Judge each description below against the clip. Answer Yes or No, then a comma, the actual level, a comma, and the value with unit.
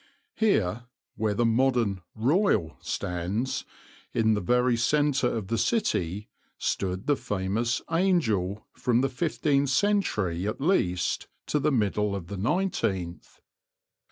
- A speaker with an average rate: No, slow, 125 wpm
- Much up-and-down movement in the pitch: Yes, wide, 6.0 semitones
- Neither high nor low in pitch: No, low, 115 Hz